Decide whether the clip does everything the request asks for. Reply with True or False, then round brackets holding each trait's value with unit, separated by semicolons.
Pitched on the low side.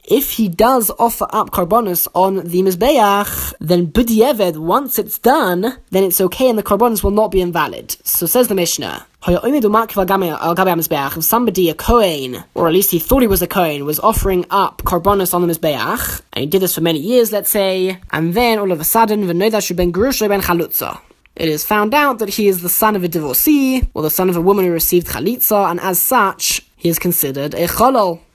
False (190 Hz)